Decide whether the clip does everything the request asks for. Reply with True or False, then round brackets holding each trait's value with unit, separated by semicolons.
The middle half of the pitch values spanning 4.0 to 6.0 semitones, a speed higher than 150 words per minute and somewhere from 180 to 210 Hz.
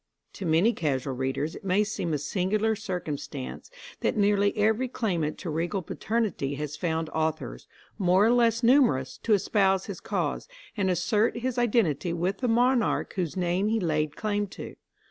True (5.5 semitones; 165 wpm; 190 Hz)